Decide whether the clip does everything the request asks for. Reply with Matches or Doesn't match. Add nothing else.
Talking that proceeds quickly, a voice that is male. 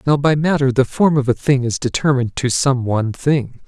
Matches